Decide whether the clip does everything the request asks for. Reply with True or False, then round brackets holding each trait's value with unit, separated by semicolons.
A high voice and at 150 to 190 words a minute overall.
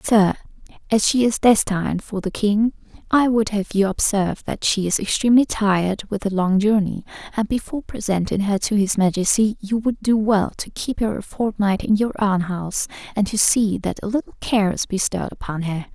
False (205 Hz; 200 wpm)